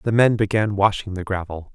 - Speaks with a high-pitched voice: No, low, 100 Hz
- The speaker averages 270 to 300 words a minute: No, fast, 205 wpm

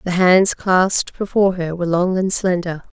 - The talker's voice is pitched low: No, medium, 180 Hz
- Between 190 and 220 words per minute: No, average, 180 wpm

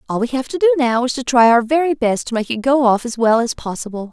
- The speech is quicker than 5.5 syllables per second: Yes, 6.2 syllables/s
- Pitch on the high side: Yes, high, 245 Hz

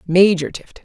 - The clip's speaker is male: No, female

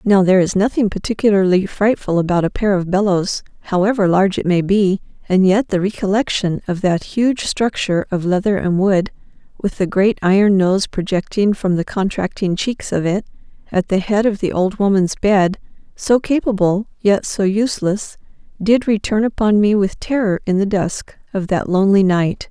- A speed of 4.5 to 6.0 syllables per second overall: Yes, 5.0 syllables/s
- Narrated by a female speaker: Yes, female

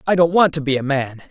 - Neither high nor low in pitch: Yes, medium, 150 Hz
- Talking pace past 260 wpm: Yes, fast, 320 wpm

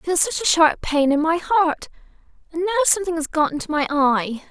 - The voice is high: Yes, very high, 325 Hz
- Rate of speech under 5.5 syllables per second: No, 6.7 syllables/s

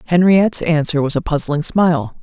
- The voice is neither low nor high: Yes, medium, 160 Hz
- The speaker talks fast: No, average, 160 wpm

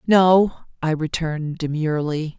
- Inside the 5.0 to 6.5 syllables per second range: No, 4.6 syllables/s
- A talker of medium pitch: Yes, medium, 160 Hz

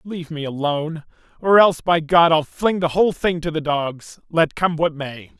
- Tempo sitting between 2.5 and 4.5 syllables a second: No, 5.0 syllables/s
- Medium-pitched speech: Yes, medium, 160 Hz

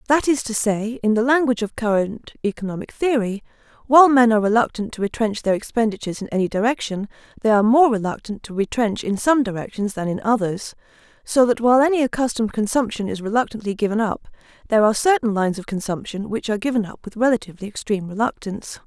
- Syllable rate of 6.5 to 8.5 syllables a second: Yes, 6.7 syllables/s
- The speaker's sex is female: Yes, female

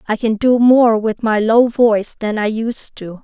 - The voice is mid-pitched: No, high, 225 Hz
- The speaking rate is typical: No, fast, 225 wpm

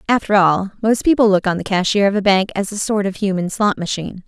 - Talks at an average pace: No, fast, 255 wpm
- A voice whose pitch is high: Yes, high, 200 Hz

